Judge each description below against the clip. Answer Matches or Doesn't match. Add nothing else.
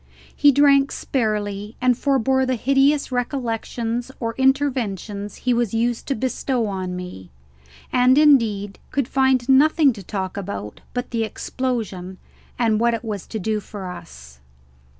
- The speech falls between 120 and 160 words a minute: Matches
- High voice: Matches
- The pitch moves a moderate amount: Matches